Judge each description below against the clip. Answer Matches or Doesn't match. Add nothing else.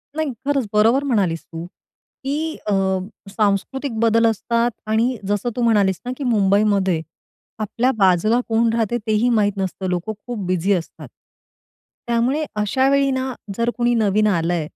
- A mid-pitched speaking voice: Doesn't match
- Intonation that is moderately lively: Matches